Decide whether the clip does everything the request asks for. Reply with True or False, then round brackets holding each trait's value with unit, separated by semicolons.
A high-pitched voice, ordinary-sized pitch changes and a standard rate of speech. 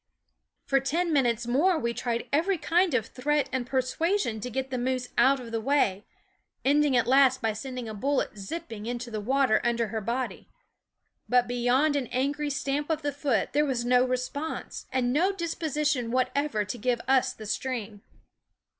True (260 Hz; 3.4 semitones; 180 wpm)